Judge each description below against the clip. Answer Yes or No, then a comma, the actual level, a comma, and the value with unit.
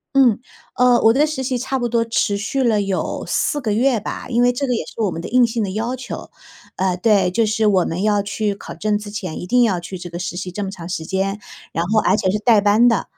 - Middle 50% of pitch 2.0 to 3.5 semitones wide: No, average, 4.0 semitones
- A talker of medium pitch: No, high, 215 Hz